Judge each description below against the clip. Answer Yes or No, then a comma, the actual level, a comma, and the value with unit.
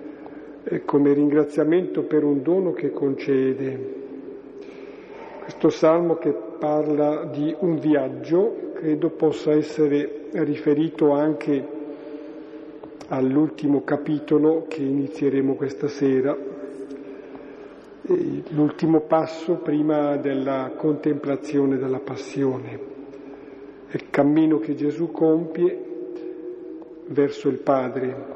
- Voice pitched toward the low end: No, medium, 150 Hz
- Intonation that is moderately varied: No, narrow, 2.1 semitones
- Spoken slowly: Yes, slow, 85 wpm